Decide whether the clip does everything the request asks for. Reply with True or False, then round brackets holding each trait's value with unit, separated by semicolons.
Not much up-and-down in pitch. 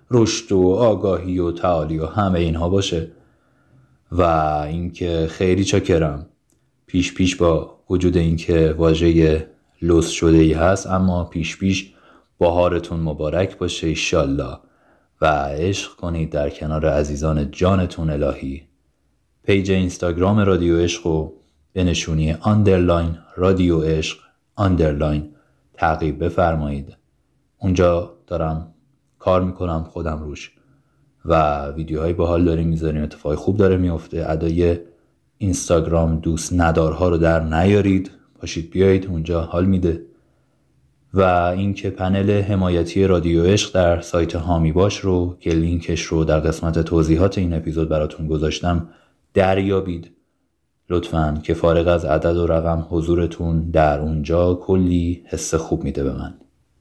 True (2.3 semitones)